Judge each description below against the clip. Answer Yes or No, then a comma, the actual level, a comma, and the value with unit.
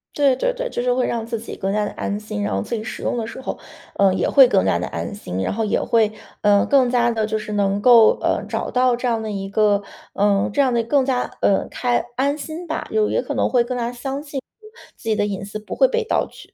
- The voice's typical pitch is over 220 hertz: Yes, high, 235 Hz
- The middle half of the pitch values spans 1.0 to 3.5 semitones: No, average, 3.9 semitones